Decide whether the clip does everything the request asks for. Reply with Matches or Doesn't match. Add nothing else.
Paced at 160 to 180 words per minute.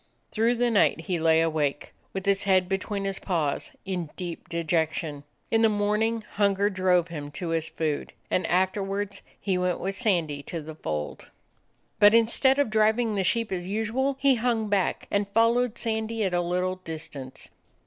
Matches